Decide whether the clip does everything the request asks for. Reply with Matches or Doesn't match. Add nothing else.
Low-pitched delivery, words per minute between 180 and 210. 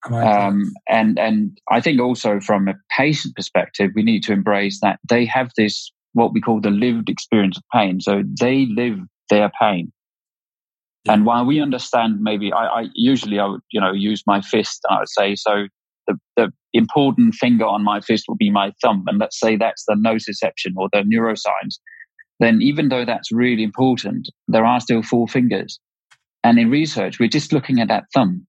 Matches